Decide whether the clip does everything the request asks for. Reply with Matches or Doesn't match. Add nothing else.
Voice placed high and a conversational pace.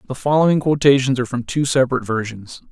Doesn't match